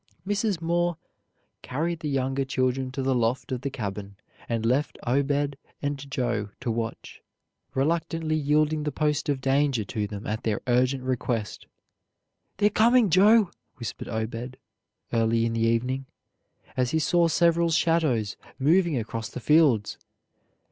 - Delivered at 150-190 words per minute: No, average, 140 wpm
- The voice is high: No, low, 135 Hz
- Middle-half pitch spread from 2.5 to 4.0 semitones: No, average, 5.2 semitones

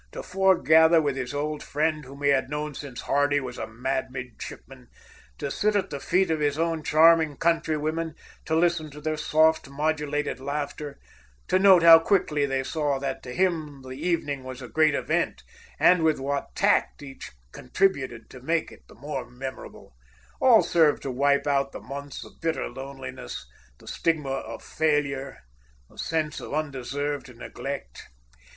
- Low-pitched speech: No, medium, 145 Hz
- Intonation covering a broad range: No, average, 3.0 semitones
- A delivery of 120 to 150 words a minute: No, average, 165 wpm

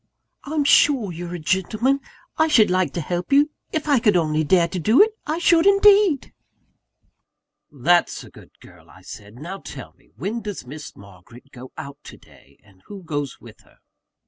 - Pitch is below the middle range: No, medium, 185 Hz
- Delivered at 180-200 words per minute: Yes, average, 185 wpm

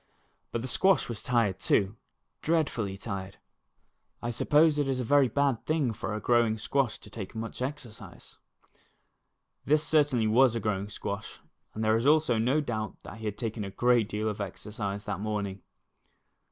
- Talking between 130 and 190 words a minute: Yes, average, 170 wpm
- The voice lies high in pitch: No, low, 115 Hz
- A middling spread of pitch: Yes, average, 4.2 semitones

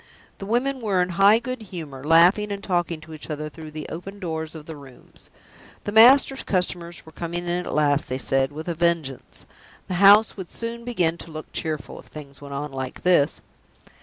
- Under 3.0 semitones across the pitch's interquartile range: No, average, 4.6 semitones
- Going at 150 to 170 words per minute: No, average, 200 wpm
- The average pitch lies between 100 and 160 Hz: No, medium, 170 Hz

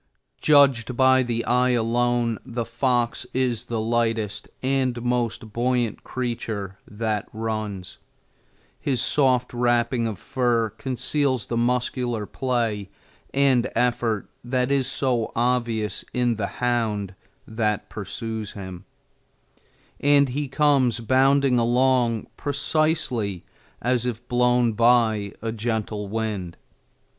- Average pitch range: No, narrow, 2.3 semitones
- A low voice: Yes, low, 120 Hz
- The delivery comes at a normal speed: No, slow, 110 wpm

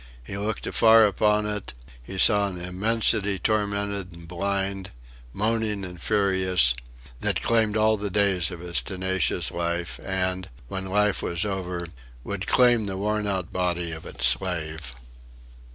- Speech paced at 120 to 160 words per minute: Yes, average, 150 wpm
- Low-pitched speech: Yes, very low, 95 Hz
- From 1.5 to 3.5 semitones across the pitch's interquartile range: Yes, average, 2.8 semitones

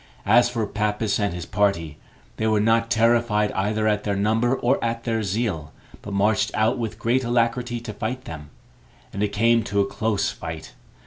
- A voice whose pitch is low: Yes, low, 110 Hz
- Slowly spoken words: No, average, 185 wpm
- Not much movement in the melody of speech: Yes, narrow, 2.3 semitones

